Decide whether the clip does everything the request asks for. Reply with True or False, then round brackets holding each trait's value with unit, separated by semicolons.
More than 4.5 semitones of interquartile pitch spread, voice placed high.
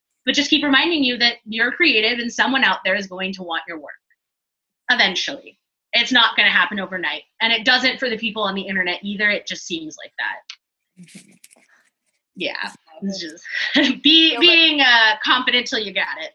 True (5.5 semitones; 230 Hz)